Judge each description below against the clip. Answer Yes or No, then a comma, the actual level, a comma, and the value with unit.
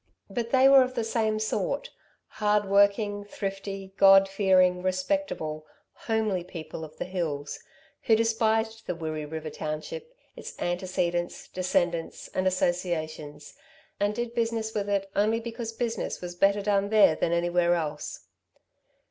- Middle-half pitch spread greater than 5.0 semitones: No, average, 4.2 semitones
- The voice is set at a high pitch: Yes, high, 195 Hz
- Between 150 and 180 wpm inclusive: No, slow, 135 wpm